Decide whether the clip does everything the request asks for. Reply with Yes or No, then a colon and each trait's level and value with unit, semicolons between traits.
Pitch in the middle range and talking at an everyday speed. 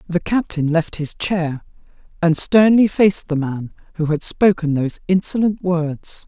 Yes: medium, 170 Hz; average, 155 wpm